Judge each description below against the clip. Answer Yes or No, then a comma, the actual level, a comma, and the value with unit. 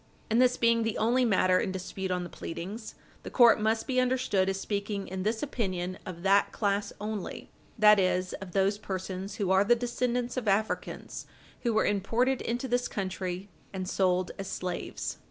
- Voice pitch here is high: Yes, high, 200 Hz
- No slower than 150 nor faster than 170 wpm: No, average, 180 wpm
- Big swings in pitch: No, average, 3.6 semitones